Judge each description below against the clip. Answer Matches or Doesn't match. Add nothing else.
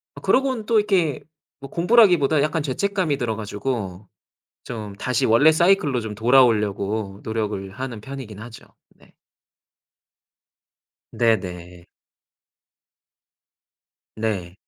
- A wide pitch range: Matches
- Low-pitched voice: Matches